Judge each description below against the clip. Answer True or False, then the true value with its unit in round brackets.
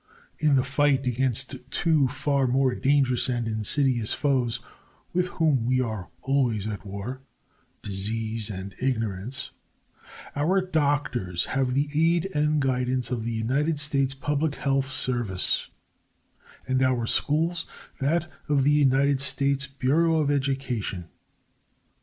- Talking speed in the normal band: False (125 wpm)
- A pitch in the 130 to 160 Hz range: True (135 Hz)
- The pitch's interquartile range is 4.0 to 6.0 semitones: False (3.4 semitones)